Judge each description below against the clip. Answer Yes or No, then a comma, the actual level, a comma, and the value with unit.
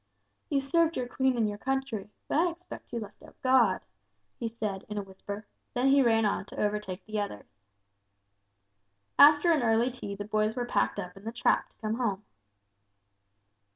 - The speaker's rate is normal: Yes, average, 180 wpm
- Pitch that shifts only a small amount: No, average, 4.3 semitones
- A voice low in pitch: No, high, 225 Hz